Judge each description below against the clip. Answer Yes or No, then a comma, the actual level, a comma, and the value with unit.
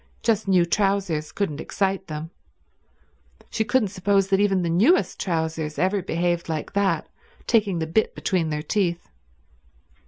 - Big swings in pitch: No, average, 3.5 semitones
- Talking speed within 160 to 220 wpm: No, average, 145 wpm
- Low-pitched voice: No, medium, 185 Hz